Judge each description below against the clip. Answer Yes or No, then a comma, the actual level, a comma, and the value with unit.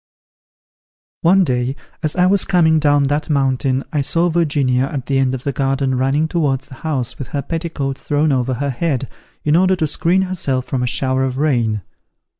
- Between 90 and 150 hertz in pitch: Yes, medium, 140 Hz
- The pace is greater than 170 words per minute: Yes, average, 190 wpm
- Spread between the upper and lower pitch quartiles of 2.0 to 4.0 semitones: Yes, average, 3.3 semitones